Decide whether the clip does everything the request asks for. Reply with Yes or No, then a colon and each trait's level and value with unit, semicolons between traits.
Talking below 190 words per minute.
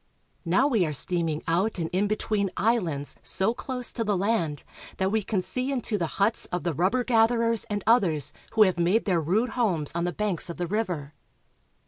No: average, 195 wpm